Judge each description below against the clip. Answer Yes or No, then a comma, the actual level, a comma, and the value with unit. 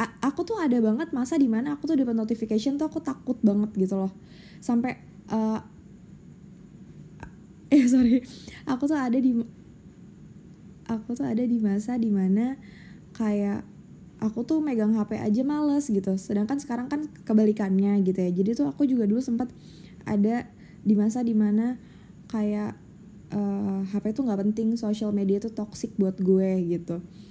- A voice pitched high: Yes, high, 220 Hz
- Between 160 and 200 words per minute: No, average, 150 wpm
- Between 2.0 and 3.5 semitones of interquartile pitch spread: No, average, 4.1 semitones